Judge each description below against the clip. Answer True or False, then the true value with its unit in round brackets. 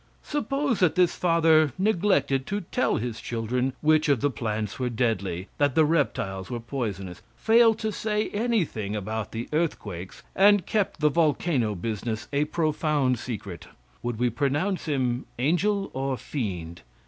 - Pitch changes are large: True (7.3 semitones)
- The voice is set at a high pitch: False (140 Hz)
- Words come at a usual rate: True (150 wpm)